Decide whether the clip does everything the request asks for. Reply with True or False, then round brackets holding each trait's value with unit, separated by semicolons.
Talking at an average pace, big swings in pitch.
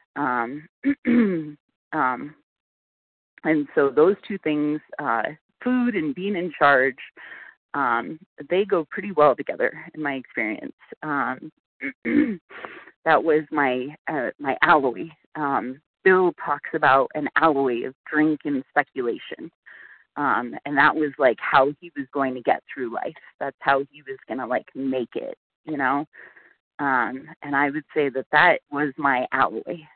False (145 wpm; 4.6 semitones)